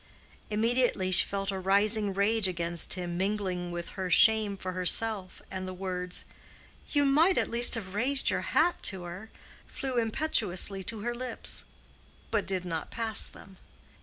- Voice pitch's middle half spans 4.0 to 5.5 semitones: No, average, 3.5 semitones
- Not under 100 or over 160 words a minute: Yes, average, 155 wpm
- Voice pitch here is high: Yes, high, 200 Hz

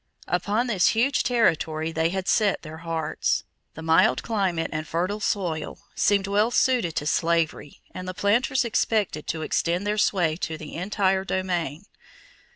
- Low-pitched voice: No, medium, 185 Hz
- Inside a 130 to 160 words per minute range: Yes, average, 155 wpm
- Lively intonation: No, average, 4.3 semitones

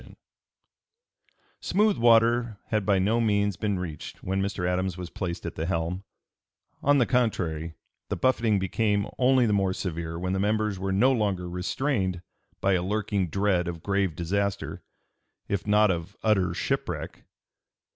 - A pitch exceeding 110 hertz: No, low, 100 Hz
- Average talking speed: Yes, average, 155 wpm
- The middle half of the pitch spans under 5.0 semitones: Yes, average, 3.1 semitones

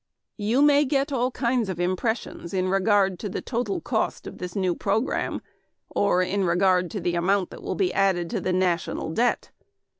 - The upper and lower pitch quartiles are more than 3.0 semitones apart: Yes, average, 4.2 semitones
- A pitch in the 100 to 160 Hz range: No, high, 195 Hz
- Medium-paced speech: Yes, average, 190 wpm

